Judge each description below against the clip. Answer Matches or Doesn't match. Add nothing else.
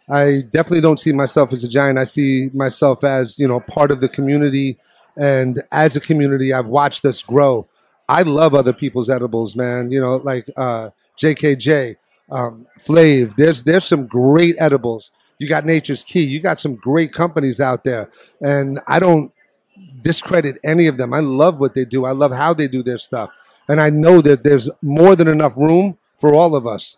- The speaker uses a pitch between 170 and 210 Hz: Doesn't match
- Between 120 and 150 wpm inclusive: Doesn't match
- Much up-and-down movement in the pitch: Doesn't match